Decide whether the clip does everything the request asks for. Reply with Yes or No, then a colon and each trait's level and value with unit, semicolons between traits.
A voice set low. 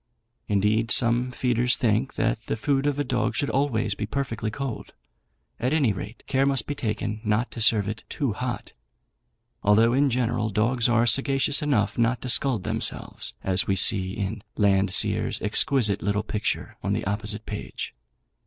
Yes: low, 115 Hz